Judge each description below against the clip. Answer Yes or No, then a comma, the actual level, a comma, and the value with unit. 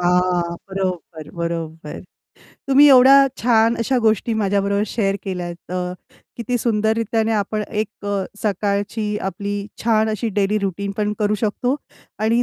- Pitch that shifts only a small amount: No, average, 3.0 semitones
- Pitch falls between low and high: No, high, 205 Hz